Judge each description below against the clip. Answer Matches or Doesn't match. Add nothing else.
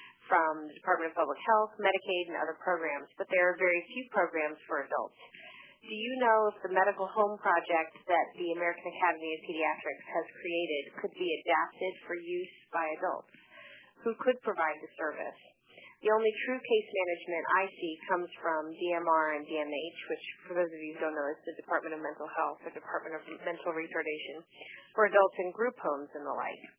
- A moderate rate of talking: Matches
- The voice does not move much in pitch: Doesn't match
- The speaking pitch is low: Doesn't match